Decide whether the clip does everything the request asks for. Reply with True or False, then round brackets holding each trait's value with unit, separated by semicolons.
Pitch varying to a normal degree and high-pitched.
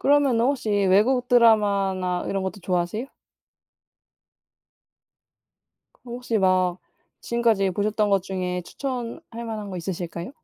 True (4.1 semitones; 205 Hz)